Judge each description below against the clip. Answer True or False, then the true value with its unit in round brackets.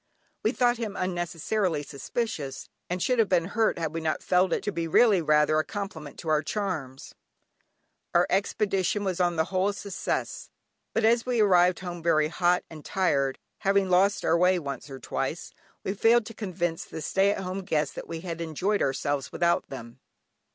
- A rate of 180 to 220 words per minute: True (185 wpm)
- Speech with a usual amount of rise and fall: True (4.0 semitones)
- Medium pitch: True (180 Hz)